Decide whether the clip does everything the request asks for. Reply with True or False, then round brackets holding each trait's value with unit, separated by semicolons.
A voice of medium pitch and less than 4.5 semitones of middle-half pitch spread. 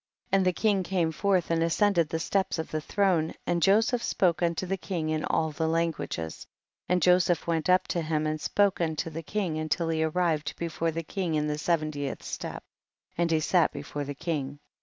True (165 Hz; 2.6 semitones)